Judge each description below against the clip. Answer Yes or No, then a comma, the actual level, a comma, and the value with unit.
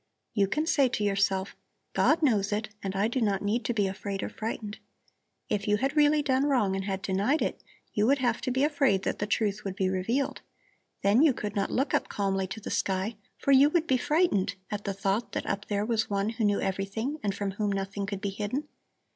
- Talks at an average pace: No, fast, 230 wpm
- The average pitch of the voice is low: No, high, 210 Hz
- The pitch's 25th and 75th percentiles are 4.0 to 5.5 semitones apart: Yes, average, 4.6 semitones